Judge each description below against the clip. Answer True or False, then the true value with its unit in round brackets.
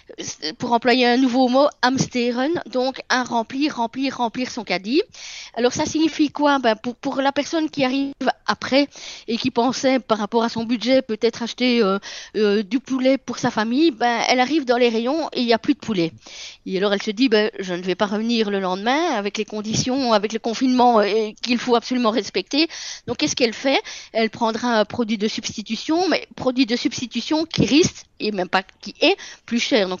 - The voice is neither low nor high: False (245 Hz)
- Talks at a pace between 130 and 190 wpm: False (205 wpm)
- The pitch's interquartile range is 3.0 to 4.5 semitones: True (3.3 semitones)